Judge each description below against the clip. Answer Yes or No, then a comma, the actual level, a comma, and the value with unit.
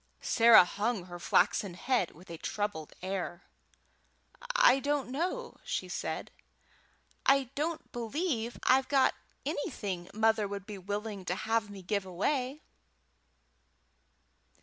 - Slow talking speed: Yes, slow, 120 wpm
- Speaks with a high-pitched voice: Yes, high, 220 Hz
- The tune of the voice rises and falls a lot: Yes, wide, 5.8 semitones